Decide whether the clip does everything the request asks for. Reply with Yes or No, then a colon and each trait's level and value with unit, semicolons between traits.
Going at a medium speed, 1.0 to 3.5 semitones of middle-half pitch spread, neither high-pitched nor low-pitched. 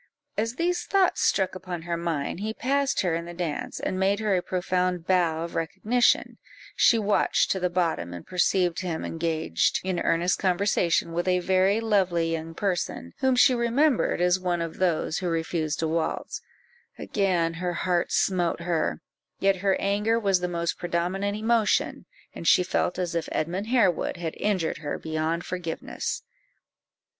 Yes: average, 165 wpm; average, 2.9 semitones; medium, 180 Hz